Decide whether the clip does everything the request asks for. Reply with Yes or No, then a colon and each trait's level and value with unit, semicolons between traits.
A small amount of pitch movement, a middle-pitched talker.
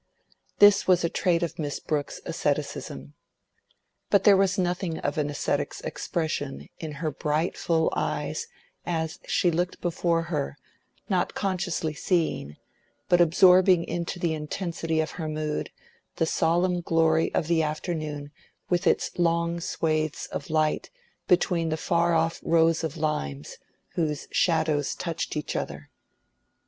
Yes: narrow, 2.1 semitones; medium, 165 Hz